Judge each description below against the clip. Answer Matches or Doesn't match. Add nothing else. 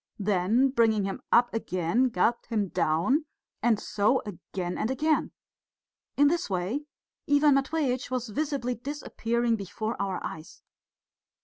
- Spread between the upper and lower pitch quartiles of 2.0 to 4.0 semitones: Doesn't match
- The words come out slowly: Matches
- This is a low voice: Doesn't match